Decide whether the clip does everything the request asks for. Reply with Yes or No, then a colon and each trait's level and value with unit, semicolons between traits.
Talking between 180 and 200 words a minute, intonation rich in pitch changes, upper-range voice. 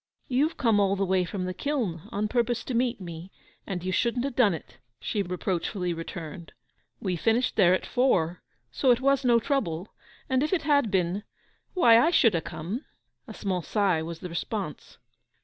Yes: average, 185 wpm; wide, 5.7 semitones; high, 200 Hz